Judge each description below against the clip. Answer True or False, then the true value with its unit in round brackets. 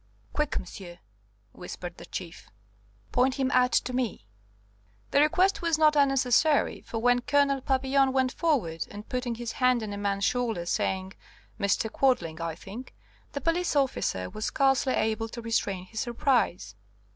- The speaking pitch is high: True (245 Hz)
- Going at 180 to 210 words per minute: False (155 wpm)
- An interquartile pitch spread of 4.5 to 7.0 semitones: True (5.3 semitones)